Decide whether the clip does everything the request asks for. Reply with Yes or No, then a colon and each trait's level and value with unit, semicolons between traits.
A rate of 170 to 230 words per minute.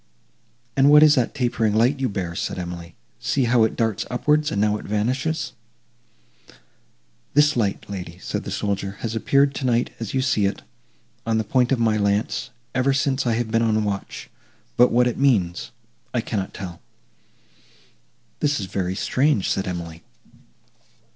No: average, 160 wpm